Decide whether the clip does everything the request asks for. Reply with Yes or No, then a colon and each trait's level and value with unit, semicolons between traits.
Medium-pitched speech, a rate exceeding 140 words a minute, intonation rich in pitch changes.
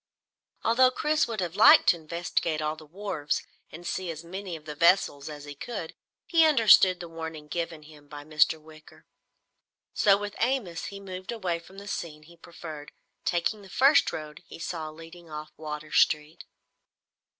No: medium, 170 Hz; average, 175 wpm; average, 4.2 semitones